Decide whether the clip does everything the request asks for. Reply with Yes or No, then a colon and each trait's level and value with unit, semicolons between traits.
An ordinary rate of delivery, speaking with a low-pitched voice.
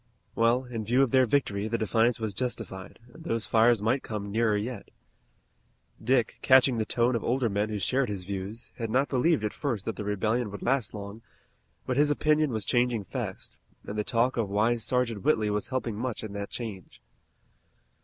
Yes: average, 195 wpm; low, 115 Hz